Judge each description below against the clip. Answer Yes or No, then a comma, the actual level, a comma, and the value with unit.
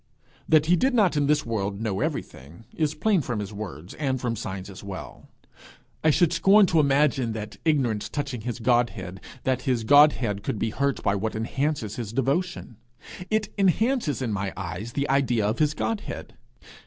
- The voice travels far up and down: Yes, wide, 6.1 semitones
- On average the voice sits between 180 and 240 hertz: No, low, 125 Hz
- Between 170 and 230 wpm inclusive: Yes, average, 180 wpm